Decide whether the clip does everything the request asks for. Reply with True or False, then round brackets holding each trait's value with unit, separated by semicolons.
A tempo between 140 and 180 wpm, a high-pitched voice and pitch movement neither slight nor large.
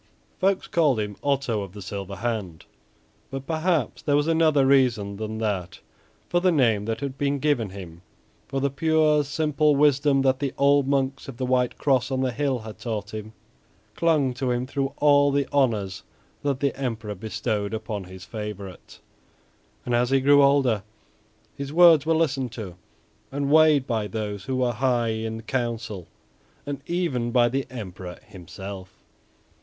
False (165 wpm; 130 Hz; 4.7 semitones)